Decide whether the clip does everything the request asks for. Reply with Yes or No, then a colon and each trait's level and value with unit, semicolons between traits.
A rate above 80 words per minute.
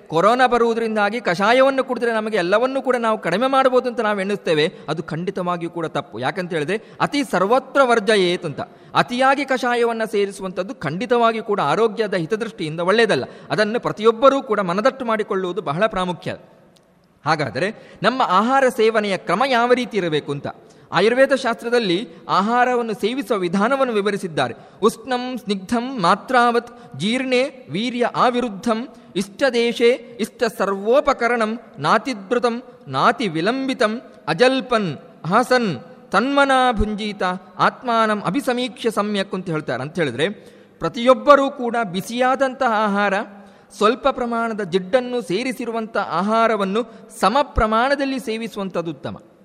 Yes: fast, 105 wpm